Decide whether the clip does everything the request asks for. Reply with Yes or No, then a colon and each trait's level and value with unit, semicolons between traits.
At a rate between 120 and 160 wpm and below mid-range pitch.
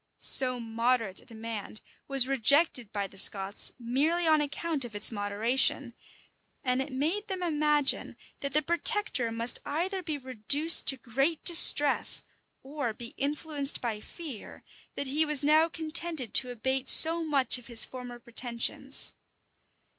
No: average, 145 wpm; very high, 270 Hz